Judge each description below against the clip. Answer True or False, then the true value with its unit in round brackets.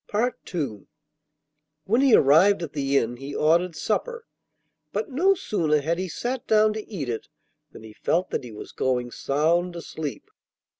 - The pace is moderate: True (160 wpm)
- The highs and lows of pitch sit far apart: True (7.4 semitones)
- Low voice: False (165 Hz)